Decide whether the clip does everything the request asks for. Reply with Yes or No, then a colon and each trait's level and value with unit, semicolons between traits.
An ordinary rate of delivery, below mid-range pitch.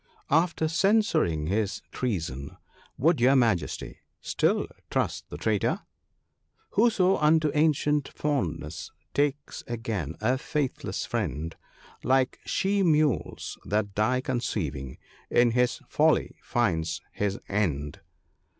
No: slow, 110 wpm; low, 120 Hz